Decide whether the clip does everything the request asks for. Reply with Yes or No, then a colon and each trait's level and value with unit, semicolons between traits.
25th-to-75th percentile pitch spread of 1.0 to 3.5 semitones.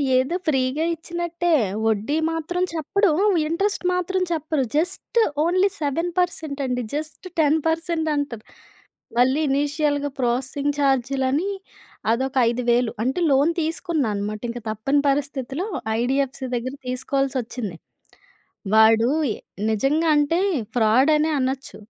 No: average, 4.2 semitones